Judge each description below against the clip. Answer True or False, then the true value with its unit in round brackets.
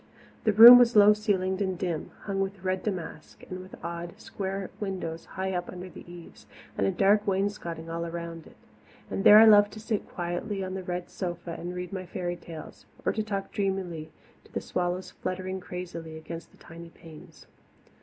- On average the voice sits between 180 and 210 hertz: True (185 Hz)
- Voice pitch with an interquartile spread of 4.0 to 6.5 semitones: False (2.5 semitones)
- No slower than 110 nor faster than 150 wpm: False (185 wpm)